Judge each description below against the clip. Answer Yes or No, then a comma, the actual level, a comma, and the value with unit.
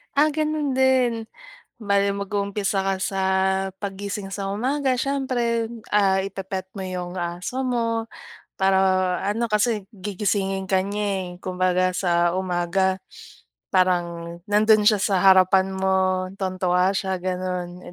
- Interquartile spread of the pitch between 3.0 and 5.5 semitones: No, narrow, 2.4 semitones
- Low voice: No, high, 195 Hz